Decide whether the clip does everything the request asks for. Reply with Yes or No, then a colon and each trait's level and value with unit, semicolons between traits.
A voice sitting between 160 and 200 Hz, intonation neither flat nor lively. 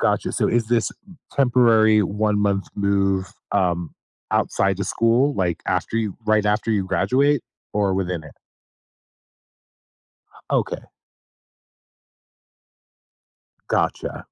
No: low, 105 Hz; average, 3.0 semitones